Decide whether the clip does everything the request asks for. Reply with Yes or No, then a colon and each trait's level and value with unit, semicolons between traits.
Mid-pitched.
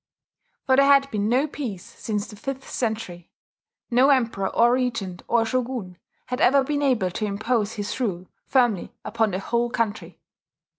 No: high, 235 Hz